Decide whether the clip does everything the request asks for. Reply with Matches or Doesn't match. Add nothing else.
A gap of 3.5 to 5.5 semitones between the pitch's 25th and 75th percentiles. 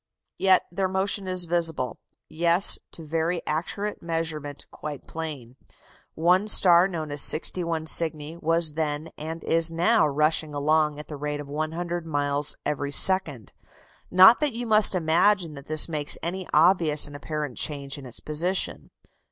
Doesn't match